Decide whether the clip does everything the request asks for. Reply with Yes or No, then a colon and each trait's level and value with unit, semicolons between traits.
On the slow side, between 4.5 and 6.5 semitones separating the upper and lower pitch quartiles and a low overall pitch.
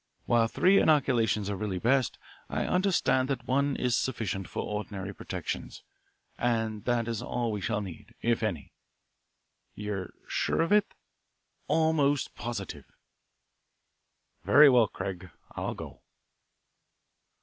Yes: slow, 120 wpm; average, 5.0 semitones; low, 115 Hz